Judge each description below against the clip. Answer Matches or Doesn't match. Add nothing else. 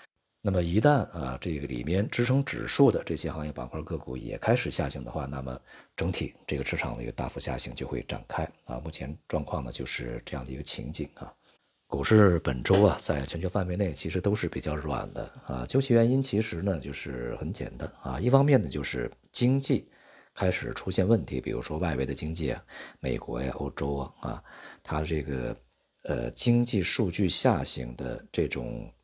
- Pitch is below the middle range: Matches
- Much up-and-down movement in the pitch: Matches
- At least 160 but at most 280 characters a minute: Doesn't match